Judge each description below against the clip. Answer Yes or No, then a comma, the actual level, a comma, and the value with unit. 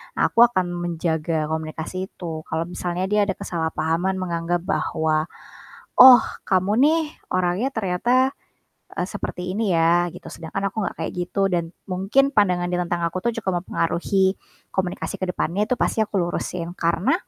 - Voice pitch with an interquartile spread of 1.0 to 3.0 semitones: Yes, average, 2.7 semitones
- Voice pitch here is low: No, medium, 180 Hz